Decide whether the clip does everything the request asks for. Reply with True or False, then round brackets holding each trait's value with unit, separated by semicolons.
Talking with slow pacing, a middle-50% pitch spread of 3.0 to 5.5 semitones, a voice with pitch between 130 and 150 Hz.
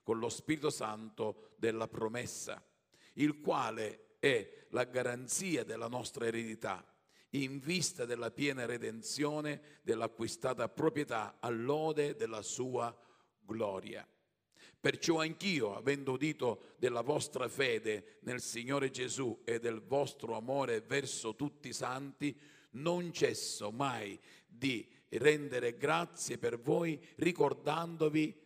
True (110 wpm; 4.6 semitones; 140 Hz)